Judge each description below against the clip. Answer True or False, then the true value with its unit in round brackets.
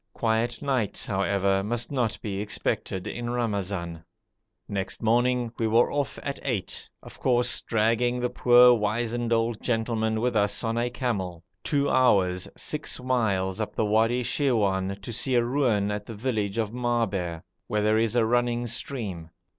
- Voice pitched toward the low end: True (115 Hz)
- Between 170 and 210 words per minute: False (160 wpm)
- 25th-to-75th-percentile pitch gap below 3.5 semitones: True (3.0 semitones)